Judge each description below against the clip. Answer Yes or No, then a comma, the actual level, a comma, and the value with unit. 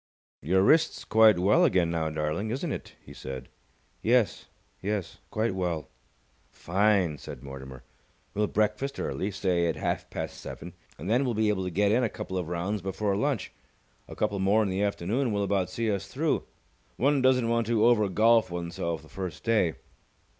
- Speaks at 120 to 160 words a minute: No, average, 180 wpm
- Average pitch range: Yes, average, 4.2 semitones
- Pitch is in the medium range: No, low, 100 Hz